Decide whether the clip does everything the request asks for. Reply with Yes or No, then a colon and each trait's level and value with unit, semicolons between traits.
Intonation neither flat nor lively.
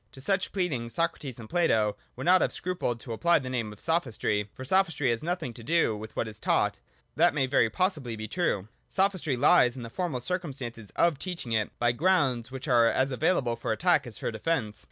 No: wide, 6.7 semitones